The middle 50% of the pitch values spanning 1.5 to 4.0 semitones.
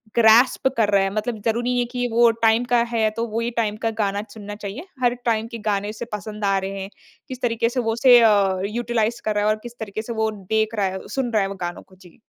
Yes: narrow, 2.4 semitones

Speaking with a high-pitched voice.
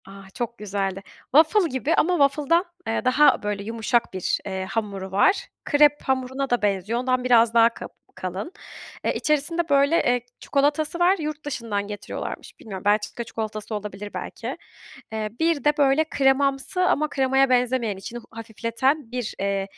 Yes: high, 245 Hz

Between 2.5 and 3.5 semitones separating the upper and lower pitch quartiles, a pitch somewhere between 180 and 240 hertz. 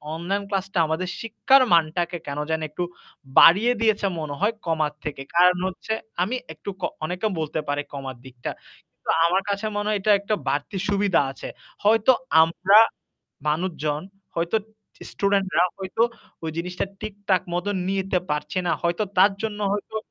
No: average, 4.2 semitones; medium, 185 Hz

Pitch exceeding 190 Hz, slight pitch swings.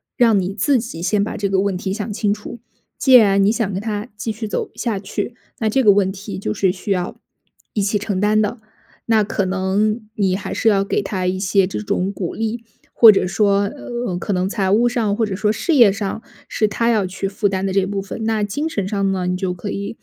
Yes: high, 200 Hz; narrow, 2.2 semitones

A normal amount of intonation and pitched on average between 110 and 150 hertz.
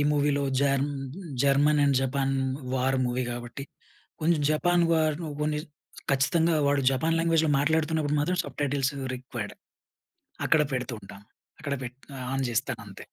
Yes: average, 3.0 semitones; medium, 140 Hz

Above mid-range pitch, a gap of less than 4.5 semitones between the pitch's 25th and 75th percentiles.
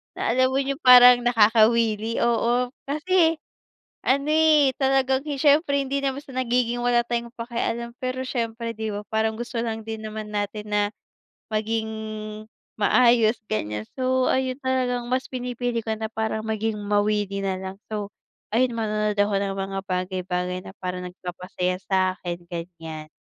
Yes: high, 230 Hz; average, 3.7 semitones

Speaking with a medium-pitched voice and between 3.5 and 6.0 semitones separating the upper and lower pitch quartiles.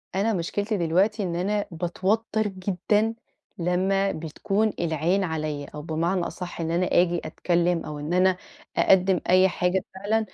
No: medium, 180 Hz; average, 2.7 semitones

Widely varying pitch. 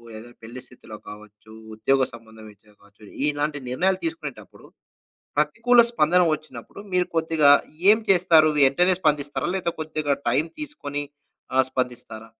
Yes: wide, 6.7 semitones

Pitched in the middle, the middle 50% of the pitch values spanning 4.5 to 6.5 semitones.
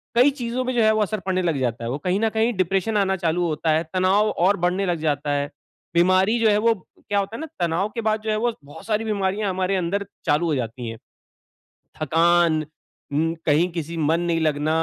Yes: medium, 180 Hz; average, 4.8 semitones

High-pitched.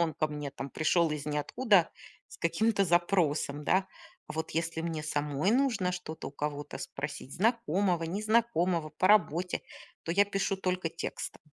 No: medium, 170 Hz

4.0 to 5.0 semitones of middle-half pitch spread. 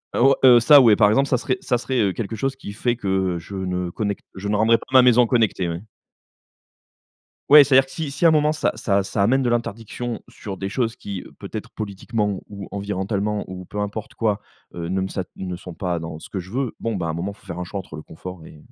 Yes: average, 4.3 semitones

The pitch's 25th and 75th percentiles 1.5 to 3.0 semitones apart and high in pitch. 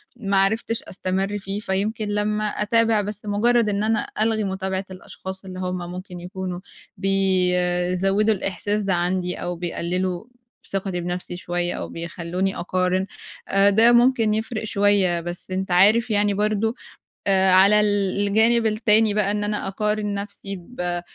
Yes: narrow, 2.5 semitones; high, 195 Hz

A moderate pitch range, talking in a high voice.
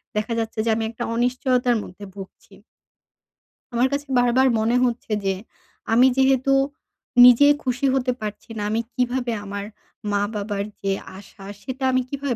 Yes: average, 3.5 semitones; high, 240 Hz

